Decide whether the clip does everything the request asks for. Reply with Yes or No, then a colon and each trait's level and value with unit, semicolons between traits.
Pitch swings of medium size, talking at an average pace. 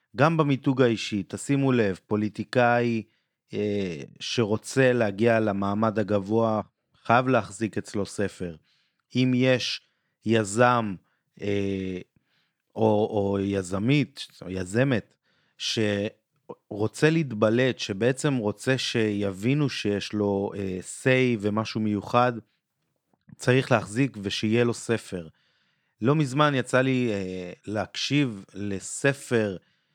No: average, 3.9 semitones; slow, 95 wpm